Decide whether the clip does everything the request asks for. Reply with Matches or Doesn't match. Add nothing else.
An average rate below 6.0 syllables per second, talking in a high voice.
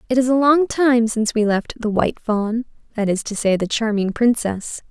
Matches